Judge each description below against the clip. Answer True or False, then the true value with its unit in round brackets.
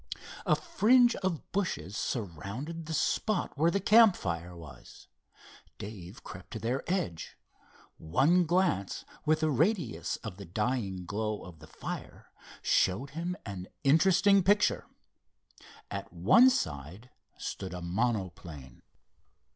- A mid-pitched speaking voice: False (120 Hz)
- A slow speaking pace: True (120 wpm)